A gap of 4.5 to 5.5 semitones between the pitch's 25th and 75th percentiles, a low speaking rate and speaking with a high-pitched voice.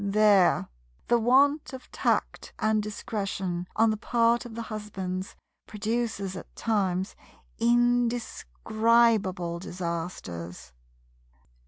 No: average, 4.1 semitones; slow, 95 wpm; high, 215 Hz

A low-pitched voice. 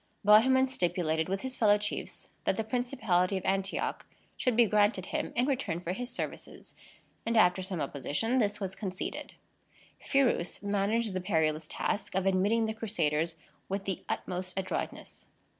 No: high, 200 Hz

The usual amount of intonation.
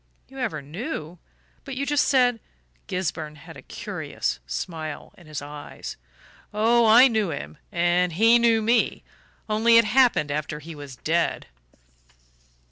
No: wide, 7.6 semitones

